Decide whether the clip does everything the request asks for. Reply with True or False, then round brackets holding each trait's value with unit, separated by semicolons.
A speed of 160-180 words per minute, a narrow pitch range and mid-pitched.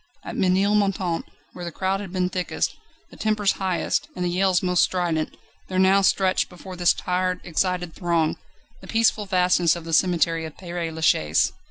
True (170 wpm; 1.8 semitones; 180 Hz)